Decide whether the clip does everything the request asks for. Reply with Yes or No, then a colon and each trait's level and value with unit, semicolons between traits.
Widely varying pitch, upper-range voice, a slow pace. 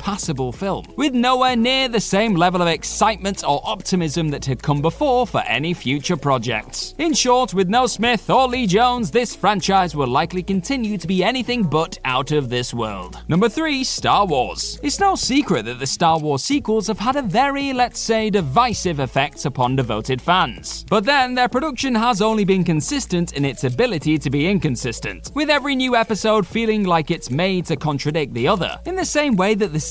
No: wide, 8.1 semitones; high, 195 Hz; average, 195 wpm